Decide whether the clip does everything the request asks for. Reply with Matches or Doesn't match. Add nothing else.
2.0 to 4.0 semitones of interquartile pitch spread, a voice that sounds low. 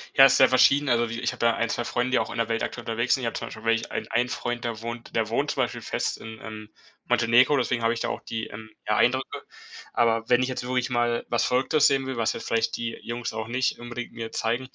Doesn't match